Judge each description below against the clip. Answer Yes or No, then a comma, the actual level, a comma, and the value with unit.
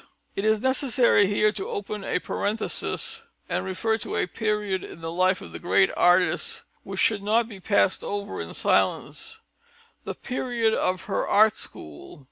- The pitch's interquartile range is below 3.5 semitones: Yes, average, 2.9 semitones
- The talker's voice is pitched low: No, high, 205 Hz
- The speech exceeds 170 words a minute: No, average, 165 wpm